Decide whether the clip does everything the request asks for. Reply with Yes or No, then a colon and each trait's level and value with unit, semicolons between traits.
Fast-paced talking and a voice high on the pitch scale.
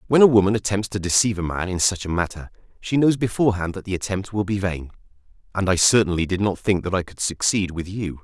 No: fast, 240 wpm; very low, 95 Hz